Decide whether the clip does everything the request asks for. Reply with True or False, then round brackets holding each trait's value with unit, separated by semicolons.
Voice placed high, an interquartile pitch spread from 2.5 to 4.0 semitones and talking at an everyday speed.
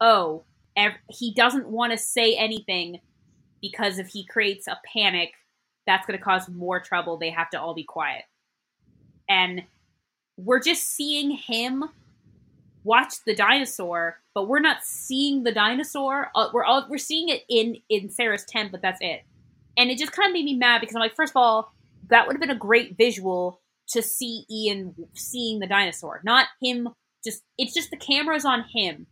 False (225 Hz; 5.4 semitones; 175 wpm)